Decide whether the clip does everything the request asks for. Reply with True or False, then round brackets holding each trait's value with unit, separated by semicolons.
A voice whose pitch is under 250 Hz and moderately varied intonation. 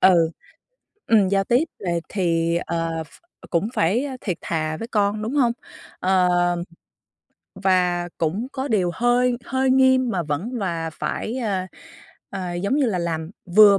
False (190 Hz; 5.7 semitones)